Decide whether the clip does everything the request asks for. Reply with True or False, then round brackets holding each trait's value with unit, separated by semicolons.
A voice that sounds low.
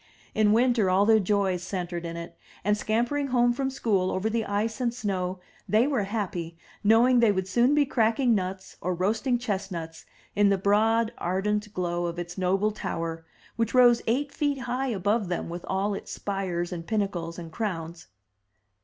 False (205 Hz)